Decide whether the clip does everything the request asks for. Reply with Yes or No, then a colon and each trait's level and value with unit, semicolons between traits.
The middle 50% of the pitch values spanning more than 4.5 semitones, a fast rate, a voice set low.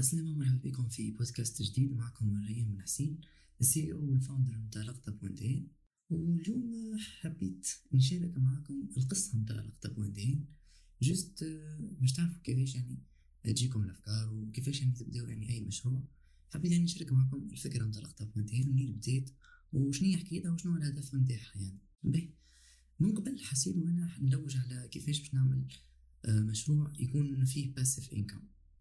Yes: wide, 5.4 semitones; fast, 145 wpm; low, 130 Hz